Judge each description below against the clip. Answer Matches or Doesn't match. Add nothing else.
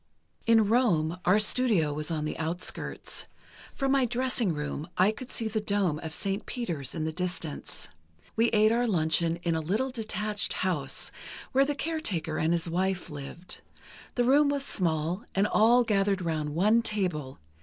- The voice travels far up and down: Matches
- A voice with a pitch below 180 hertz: Doesn't match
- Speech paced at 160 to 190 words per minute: Matches